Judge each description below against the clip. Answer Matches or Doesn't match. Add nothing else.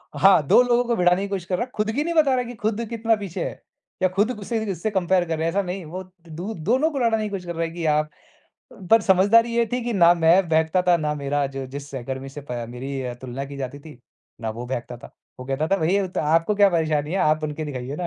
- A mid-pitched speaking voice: Matches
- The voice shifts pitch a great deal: Matches